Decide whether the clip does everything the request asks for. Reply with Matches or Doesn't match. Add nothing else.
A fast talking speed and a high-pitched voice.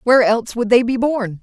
Matches